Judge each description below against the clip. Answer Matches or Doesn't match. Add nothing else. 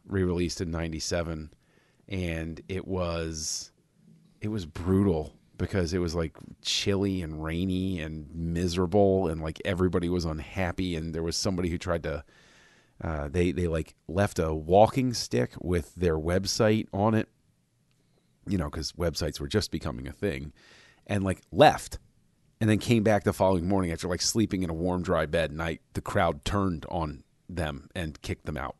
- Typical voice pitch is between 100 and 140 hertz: Doesn't match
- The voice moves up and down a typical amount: Matches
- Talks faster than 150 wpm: Matches